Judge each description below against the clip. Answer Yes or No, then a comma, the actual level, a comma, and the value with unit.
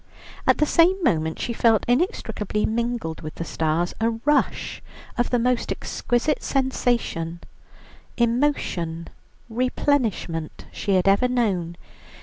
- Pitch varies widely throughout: Yes, wide, 6.6 semitones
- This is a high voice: Yes, high, 230 Hz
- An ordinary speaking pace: No, slow, 120 wpm